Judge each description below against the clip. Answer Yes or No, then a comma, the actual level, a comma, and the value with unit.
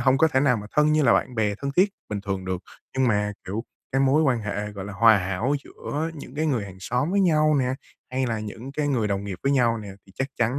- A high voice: No, low, 125 Hz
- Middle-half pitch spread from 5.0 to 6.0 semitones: Yes, wide, 5.4 semitones